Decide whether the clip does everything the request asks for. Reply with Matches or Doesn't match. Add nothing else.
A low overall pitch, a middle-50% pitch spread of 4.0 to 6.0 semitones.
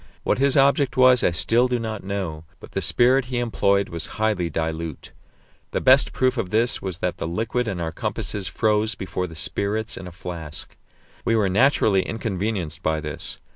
Matches